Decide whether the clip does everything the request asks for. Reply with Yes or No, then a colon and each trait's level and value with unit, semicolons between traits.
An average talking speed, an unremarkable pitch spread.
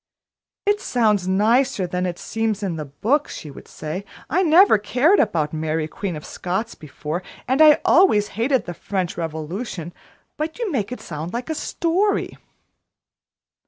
No: average, 160 wpm; wide, 8.2 semitones